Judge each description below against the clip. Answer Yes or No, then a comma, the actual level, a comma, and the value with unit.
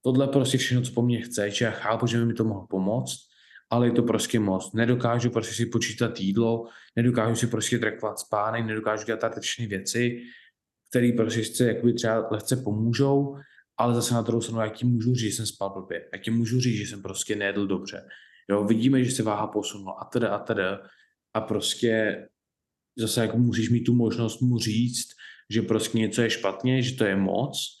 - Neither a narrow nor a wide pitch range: No, narrow, 1.9 semitones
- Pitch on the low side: Yes, low, 115 Hz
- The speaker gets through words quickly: Yes, fast, 200 wpm